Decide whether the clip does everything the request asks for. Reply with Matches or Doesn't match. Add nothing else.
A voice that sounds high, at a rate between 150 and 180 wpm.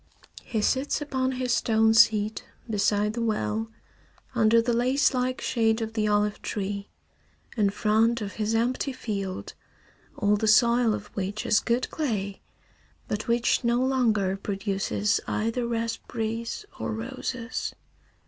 Doesn't match